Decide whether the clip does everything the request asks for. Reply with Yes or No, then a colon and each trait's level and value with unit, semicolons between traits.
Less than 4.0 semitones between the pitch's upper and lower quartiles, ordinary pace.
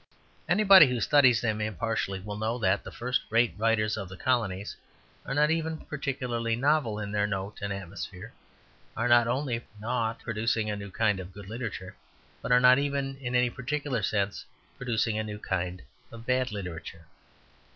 Yes: average, 3.6 semitones; average, 170 wpm